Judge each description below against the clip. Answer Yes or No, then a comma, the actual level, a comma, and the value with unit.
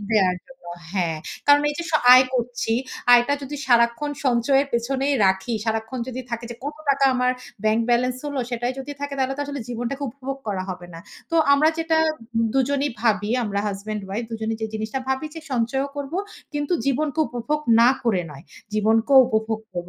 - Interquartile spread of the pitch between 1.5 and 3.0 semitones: No, average, 4.0 semitones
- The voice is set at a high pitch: Yes, high, 245 Hz